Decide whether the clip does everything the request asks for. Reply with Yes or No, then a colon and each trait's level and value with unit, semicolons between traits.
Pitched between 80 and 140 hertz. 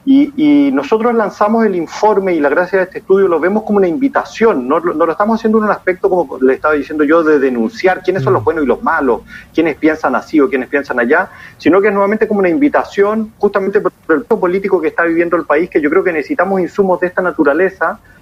No: high, 190 Hz